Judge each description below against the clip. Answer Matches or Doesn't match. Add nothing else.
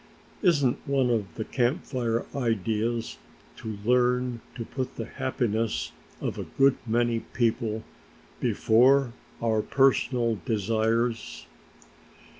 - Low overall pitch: Matches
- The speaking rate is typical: Doesn't match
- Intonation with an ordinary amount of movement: Doesn't match